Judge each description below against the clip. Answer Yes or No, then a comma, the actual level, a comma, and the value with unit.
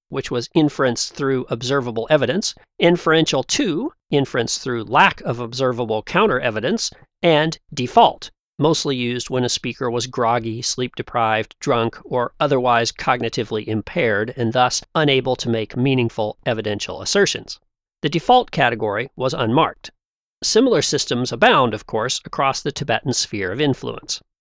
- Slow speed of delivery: Yes, slow, 130 wpm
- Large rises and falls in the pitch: No, average, 4.0 semitones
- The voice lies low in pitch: Yes, low, 125 Hz